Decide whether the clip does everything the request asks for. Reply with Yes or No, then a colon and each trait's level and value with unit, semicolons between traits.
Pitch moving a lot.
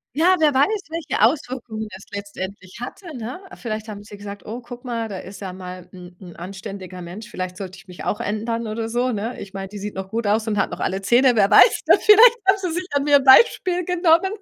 Yes: wide, 5.7 semitones